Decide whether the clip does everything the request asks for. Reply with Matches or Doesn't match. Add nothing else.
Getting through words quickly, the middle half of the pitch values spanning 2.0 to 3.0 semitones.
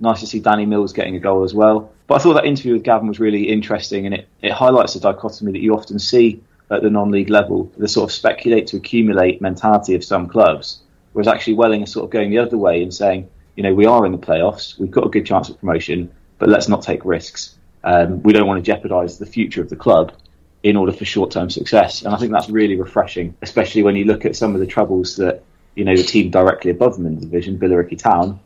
Matches